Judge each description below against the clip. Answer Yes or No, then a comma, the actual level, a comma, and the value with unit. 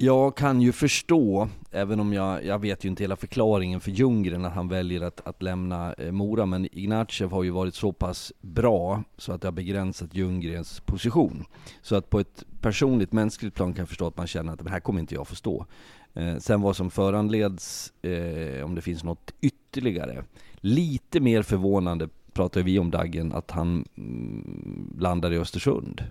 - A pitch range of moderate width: Yes, average, 3.5 semitones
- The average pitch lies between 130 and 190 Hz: No, very low, 95 Hz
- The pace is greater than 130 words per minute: Yes, average, 190 wpm